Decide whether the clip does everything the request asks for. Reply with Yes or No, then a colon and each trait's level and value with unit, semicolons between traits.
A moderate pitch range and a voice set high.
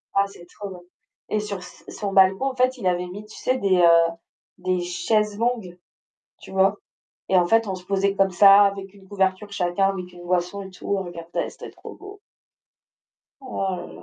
No: narrow, 2.2 semitones; high, 195 Hz